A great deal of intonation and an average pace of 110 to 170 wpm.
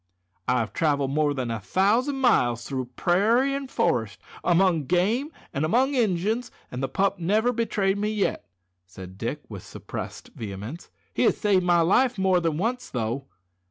Yes: wide, 8.7 semitones; average, 165 wpm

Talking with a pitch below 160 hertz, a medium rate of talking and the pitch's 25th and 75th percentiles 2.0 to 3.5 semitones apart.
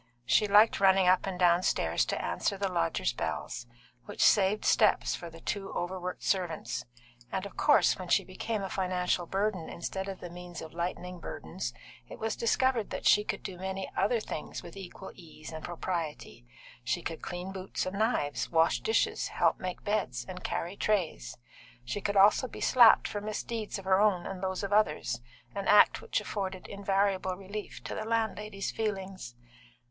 No: high, 190 Hz; average, 175 wpm; narrow, 2.6 semitones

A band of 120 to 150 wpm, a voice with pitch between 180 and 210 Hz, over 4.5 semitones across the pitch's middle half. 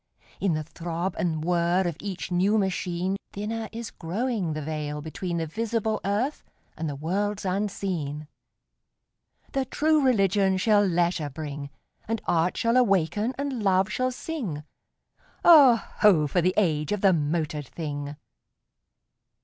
Yes: average, 140 wpm; medium, 185 Hz; average, 4.9 semitones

